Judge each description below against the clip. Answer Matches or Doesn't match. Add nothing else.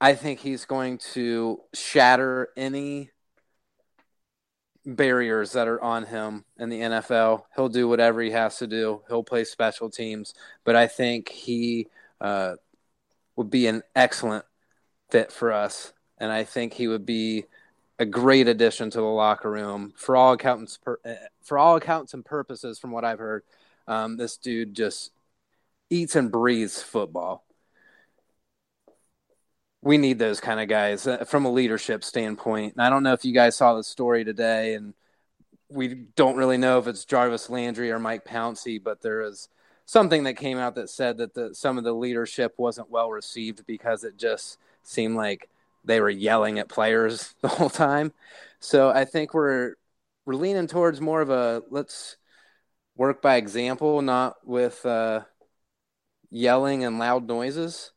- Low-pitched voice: Matches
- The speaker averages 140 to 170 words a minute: Matches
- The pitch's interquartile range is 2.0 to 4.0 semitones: Matches